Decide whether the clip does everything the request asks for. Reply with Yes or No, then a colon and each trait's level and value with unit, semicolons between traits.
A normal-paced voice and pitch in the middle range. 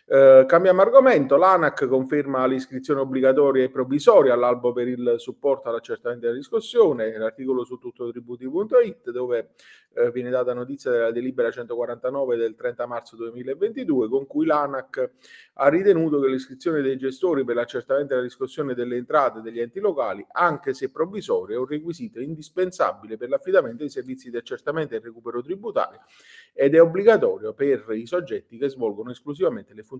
Yes: average, 160 wpm; medium, 145 Hz